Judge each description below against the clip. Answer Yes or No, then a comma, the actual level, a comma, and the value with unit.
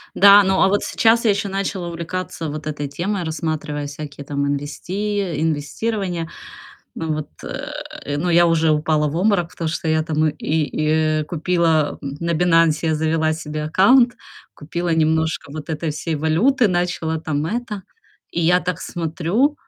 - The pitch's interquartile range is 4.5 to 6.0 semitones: No, average, 2.9 semitones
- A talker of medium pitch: Yes, medium, 160 Hz